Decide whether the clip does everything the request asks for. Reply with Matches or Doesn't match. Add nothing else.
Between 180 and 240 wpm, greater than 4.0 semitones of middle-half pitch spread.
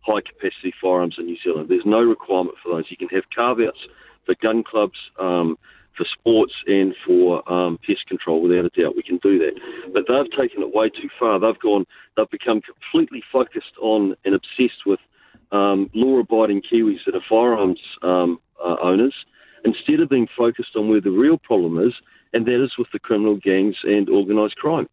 Matches